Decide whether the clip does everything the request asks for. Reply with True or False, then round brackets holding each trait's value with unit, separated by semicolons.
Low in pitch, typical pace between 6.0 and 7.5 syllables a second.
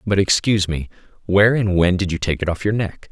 True (95 Hz; 6.2 syllables/s)